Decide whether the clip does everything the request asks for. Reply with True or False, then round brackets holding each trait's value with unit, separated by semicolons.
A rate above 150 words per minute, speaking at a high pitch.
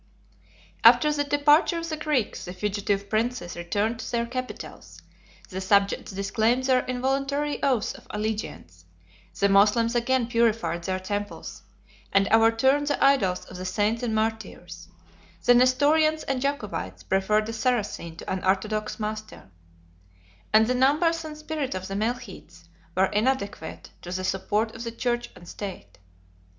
False (145 wpm; 225 Hz)